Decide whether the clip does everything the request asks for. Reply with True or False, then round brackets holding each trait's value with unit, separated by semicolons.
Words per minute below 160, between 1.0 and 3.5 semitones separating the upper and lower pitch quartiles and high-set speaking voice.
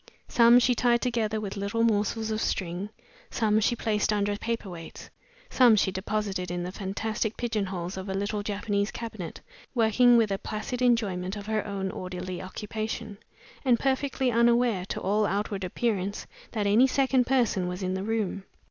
False (170 wpm; 3.2 semitones; 210 Hz)